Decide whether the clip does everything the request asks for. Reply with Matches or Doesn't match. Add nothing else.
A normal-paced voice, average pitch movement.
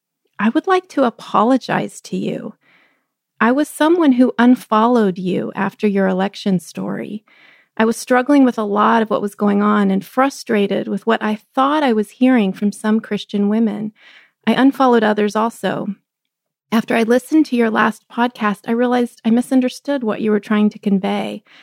Matches